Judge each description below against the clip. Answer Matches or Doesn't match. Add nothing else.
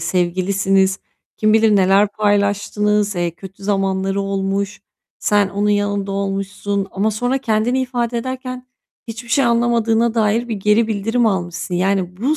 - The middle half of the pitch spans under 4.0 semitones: Matches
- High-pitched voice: Matches